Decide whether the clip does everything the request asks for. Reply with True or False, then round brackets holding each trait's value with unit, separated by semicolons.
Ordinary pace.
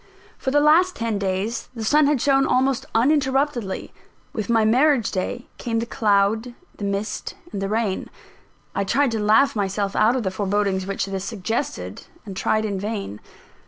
True (170 wpm)